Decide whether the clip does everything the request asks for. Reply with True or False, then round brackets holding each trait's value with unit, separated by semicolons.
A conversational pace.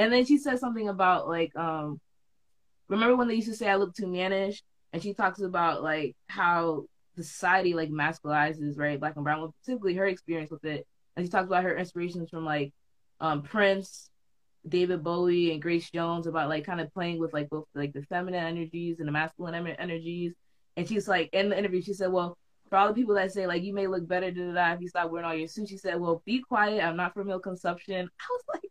False (230 wpm)